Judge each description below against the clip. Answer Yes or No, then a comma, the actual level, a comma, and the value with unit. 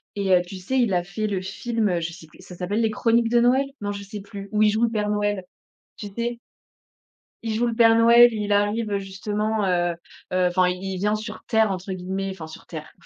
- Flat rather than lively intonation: No, average, 3.1 semitones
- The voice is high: Yes, high, 205 Hz